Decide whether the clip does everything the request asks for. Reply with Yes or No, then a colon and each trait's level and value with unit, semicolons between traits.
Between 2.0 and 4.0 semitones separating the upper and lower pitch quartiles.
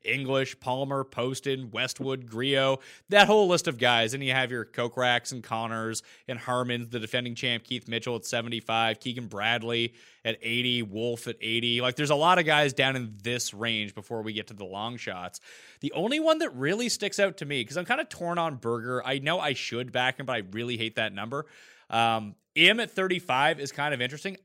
Yes: average, 3.5 semitones